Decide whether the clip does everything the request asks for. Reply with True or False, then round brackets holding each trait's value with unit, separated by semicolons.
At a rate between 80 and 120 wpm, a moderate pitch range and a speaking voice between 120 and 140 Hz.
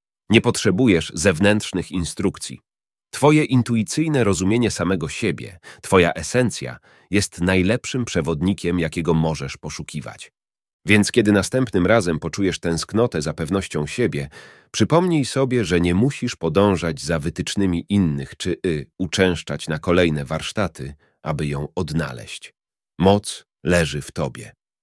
False (115 wpm; 4.8 semitones; 90 Hz)